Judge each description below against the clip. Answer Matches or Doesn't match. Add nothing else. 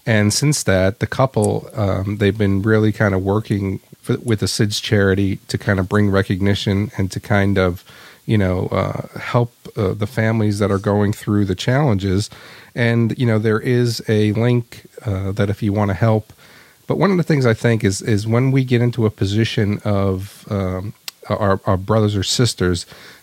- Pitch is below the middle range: Matches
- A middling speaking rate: Matches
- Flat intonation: Doesn't match